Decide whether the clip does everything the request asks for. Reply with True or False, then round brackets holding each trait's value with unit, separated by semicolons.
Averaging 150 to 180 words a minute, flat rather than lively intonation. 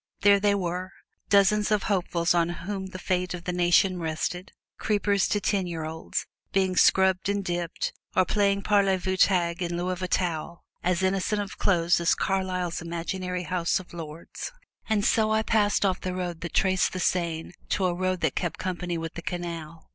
False (190 wpm; 2.1 semitones)